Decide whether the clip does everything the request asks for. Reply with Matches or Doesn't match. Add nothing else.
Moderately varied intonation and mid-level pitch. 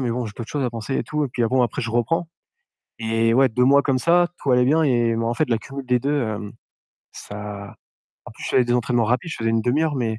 Doesn't match